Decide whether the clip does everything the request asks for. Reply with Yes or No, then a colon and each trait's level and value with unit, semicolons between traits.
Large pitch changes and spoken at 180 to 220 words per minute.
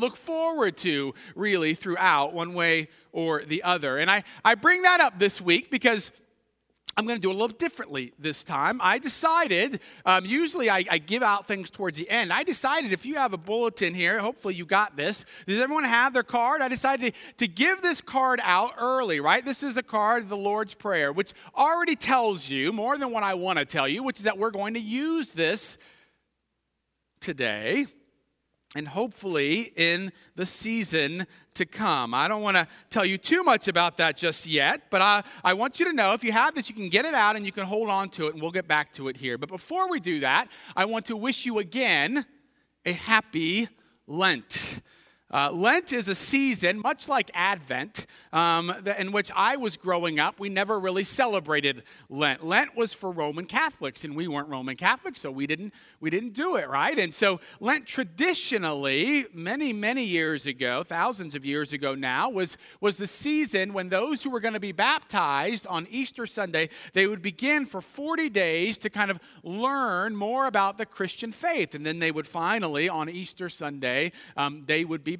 Yes: wide, 6.5 semitones; average, 200 wpm